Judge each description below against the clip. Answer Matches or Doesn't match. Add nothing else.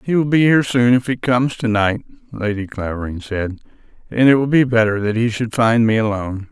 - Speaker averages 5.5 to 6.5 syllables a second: Matches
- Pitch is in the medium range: Doesn't match